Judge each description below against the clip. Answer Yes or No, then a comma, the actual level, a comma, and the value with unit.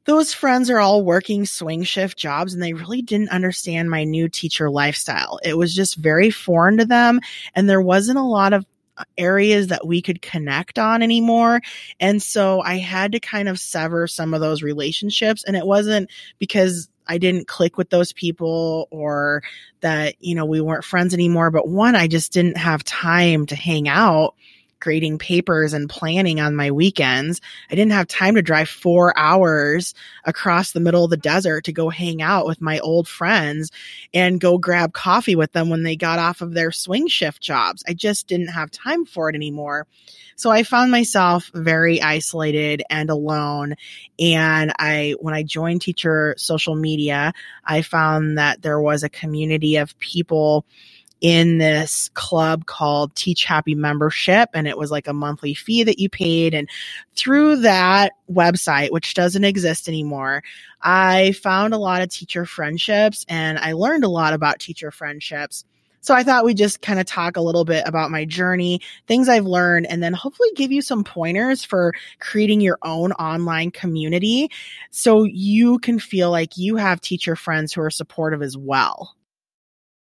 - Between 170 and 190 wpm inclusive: Yes, average, 180 wpm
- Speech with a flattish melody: No, average, 3.7 semitones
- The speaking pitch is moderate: Yes, medium, 170 Hz